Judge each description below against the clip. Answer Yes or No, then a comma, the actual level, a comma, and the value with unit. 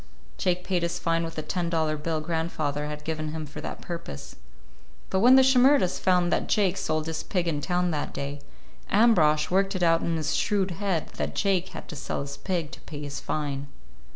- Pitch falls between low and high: Yes, medium, 165 Hz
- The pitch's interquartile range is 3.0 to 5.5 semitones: Yes, average, 3.4 semitones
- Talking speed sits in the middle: No, fast, 210 wpm